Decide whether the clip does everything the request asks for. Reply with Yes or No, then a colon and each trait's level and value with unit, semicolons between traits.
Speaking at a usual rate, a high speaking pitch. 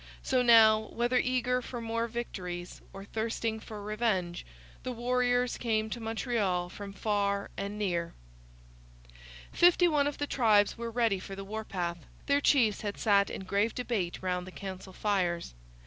Yes: average, 155 wpm; high, 220 Hz